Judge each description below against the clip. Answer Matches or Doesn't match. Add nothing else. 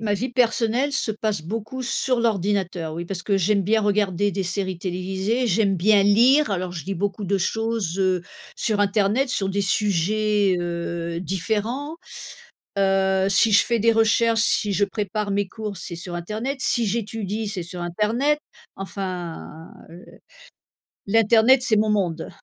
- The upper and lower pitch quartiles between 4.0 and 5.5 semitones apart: Doesn't match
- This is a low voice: Doesn't match